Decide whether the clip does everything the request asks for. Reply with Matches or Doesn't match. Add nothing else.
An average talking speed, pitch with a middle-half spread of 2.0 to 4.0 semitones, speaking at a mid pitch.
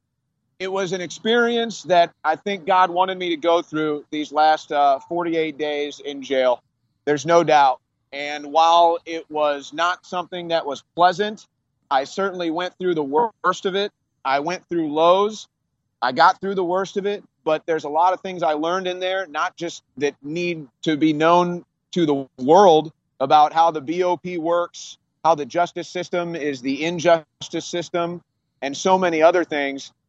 Matches